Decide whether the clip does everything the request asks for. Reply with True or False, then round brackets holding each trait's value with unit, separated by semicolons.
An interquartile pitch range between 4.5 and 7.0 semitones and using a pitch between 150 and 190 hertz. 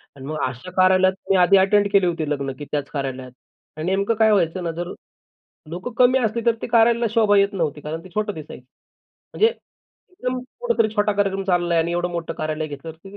True (4.8 semitones; 185 Hz)